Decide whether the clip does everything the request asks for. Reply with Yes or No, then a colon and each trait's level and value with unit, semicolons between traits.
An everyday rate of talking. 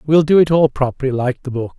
No: fast, 270 wpm